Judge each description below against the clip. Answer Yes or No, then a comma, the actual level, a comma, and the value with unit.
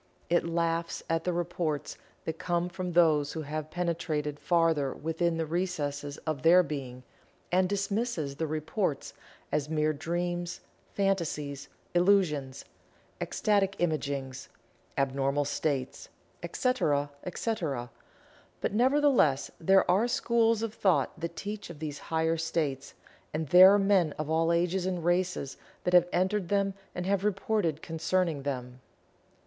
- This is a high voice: No, medium, 165 Hz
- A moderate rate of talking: No, slow, 130 wpm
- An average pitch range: Yes, average, 3.9 semitones